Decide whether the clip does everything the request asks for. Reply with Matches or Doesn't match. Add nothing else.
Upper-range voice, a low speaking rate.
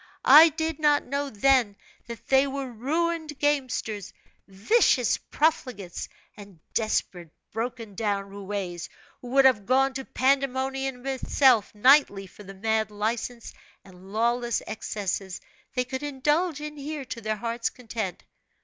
Matches